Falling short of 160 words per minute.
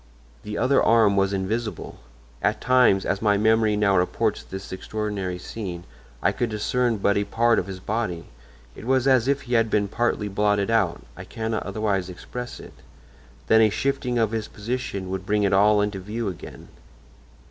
No: average, 170 wpm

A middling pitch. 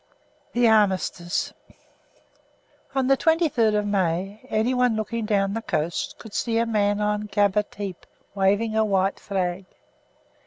No: high, 210 Hz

